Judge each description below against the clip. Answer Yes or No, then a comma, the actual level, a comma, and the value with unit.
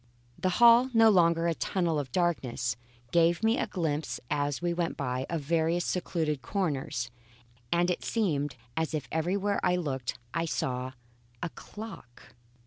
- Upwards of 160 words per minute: No, average, 150 wpm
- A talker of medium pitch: Yes, medium, 165 Hz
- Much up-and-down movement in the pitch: No, average, 3.9 semitones